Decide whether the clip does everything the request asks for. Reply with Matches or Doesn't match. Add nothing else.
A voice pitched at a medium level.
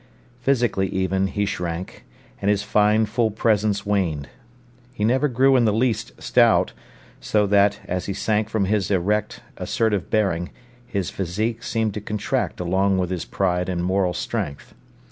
Doesn't match